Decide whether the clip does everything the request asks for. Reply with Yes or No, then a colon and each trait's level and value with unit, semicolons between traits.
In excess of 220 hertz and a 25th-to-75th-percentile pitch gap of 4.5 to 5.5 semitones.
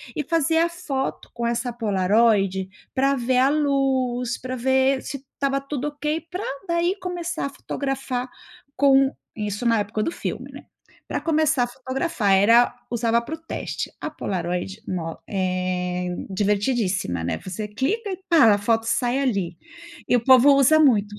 Yes: very high, 250 Hz; average, 5.2 semitones